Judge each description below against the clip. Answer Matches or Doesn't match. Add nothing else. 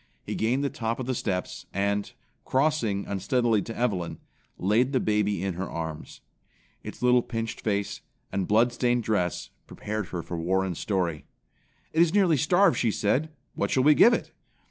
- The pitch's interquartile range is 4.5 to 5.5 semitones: Matches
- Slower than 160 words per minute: Doesn't match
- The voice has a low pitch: Matches